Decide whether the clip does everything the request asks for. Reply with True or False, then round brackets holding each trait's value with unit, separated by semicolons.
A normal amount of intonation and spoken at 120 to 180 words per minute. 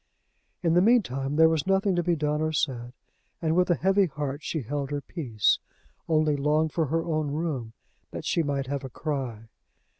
False (3.3 semitones; 200 wpm)